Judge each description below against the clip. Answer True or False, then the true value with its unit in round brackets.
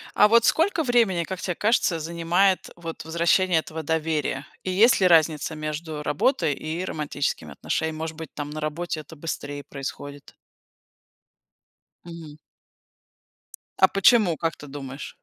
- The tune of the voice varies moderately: True (3.5 semitones)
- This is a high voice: False (160 Hz)